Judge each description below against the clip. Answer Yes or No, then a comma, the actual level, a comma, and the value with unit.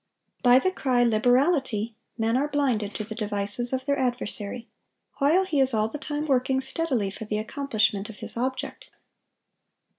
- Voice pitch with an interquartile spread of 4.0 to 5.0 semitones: Yes, average, 4.3 semitones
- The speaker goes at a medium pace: Yes, average, 160 wpm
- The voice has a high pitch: Yes, very high, 250 Hz